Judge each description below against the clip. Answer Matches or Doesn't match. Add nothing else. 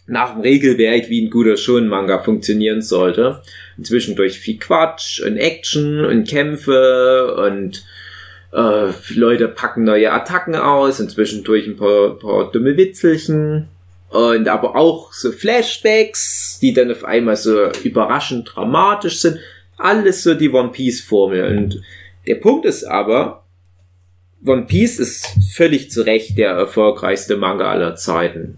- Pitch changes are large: Matches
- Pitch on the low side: Matches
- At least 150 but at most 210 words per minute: Doesn't match